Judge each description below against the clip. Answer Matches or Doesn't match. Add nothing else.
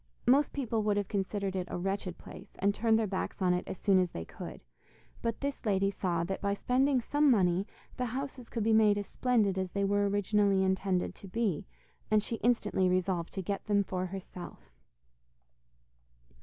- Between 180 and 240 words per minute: Matches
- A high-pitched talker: Matches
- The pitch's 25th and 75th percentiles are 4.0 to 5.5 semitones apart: Doesn't match